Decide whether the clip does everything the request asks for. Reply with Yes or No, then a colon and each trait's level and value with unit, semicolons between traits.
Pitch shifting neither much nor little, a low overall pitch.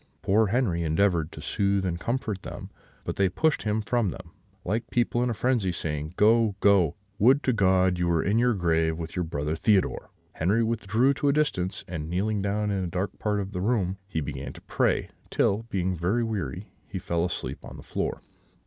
Yes: average, 4.3 semitones; low, 100 Hz